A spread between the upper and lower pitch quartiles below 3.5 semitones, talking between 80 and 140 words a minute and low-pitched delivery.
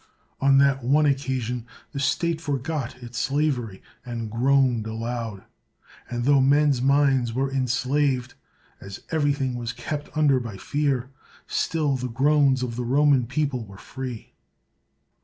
Yes: average, 2.9 semitones; slow, 135 wpm; low, 130 Hz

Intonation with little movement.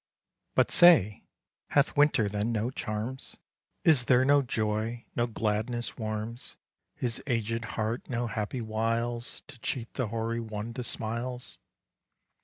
Yes: narrow, 2.2 semitones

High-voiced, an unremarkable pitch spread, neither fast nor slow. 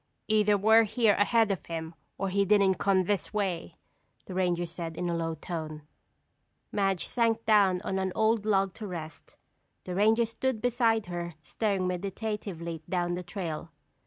Yes: high, 195 Hz; average, 3.6 semitones; average, 160 wpm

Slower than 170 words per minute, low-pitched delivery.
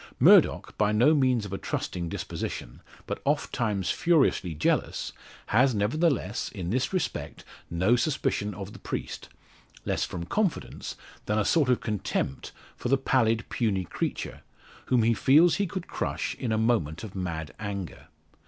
Yes: average, 155 wpm; low, 110 Hz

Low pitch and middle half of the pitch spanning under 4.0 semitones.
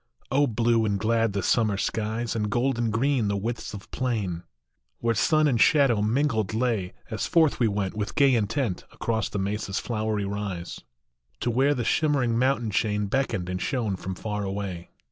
Yes: low, 110 Hz; average, 3.3 semitones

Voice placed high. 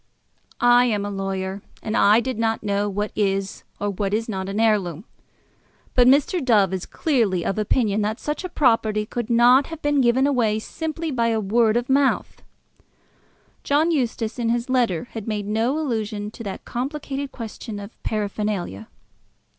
Yes: high, 225 Hz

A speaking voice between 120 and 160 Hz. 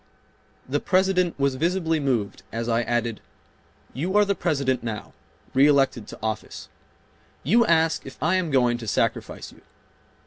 Yes: medium, 140 Hz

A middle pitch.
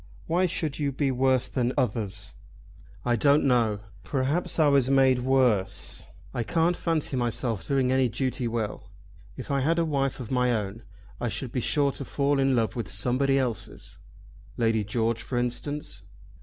No: low, 130 Hz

